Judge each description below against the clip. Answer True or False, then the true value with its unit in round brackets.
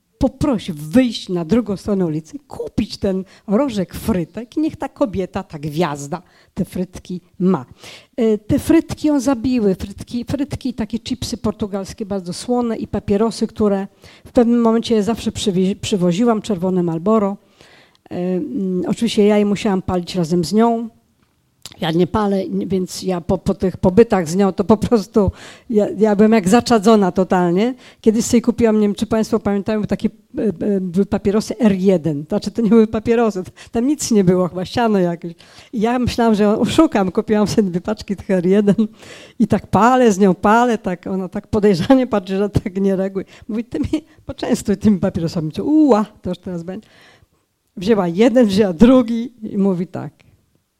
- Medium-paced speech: False (165 wpm)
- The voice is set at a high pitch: True (210 Hz)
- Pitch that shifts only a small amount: False (3.4 semitones)